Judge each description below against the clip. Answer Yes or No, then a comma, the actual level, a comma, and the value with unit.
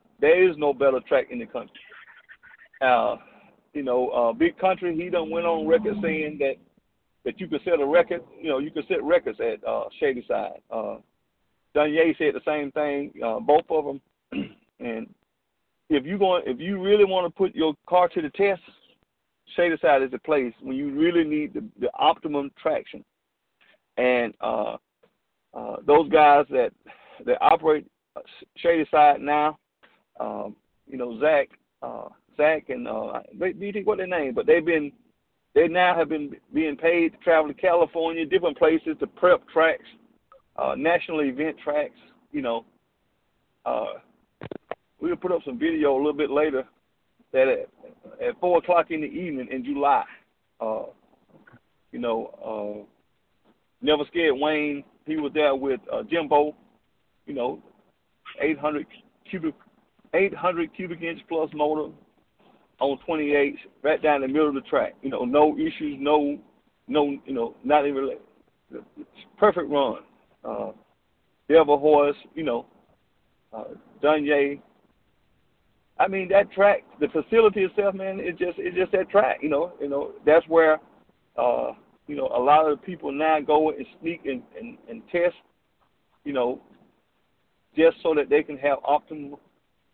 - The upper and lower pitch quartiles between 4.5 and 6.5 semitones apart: Yes, average, 4.9 semitones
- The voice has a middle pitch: Yes, medium, 160 Hz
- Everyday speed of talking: Yes, average, 160 wpm